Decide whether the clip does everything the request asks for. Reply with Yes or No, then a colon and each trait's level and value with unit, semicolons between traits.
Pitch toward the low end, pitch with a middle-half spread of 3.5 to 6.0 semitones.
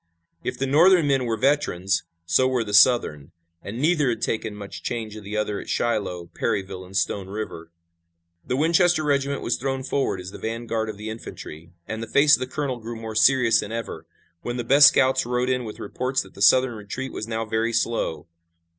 Yes: low, 115 Hz; average, 4.1 semitones